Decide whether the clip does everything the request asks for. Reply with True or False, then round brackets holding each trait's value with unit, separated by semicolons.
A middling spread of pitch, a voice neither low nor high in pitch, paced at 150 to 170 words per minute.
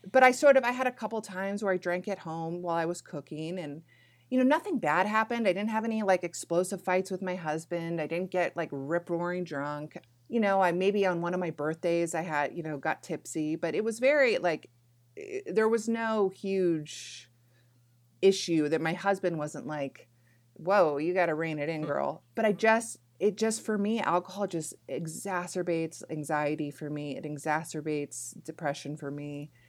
False (4.7 semitones; 170 Hz; 200 wpm)